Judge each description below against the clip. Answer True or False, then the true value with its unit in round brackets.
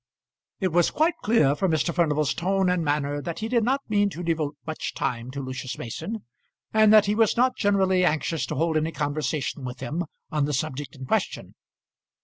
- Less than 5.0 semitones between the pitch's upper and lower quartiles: False (5.5 semitones)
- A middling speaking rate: True (195 wpm)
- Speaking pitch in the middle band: True (165 Hz)